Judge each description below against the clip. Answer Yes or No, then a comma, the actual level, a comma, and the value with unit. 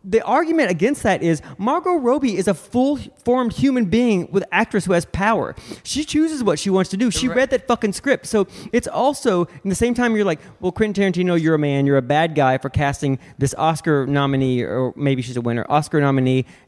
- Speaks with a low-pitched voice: No, high, 190 Hz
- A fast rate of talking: Yes, fast, 215 wpm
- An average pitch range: No, wide, 9.0 semitones